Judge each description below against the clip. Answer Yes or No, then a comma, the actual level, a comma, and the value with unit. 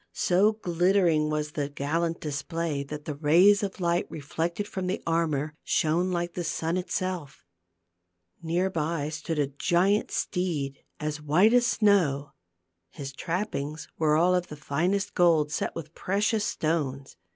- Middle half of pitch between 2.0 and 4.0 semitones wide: Yes, average, 3.4 semitones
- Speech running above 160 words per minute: No, average, 145 wpm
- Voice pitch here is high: No, medium, 165 Hz